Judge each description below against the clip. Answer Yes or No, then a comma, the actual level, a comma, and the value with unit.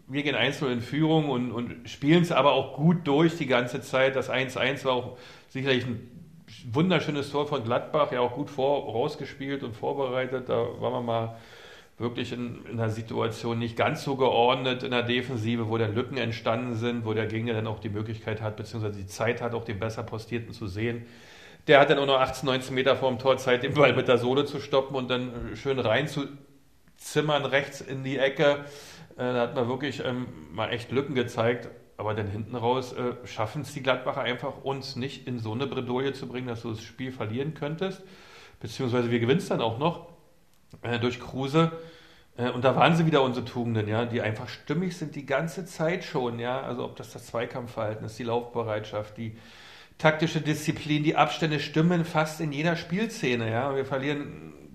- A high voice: No, low, 130 Hz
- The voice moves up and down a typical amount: Yes, average, 3.4 semitones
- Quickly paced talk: Yes, fast, 195 wpm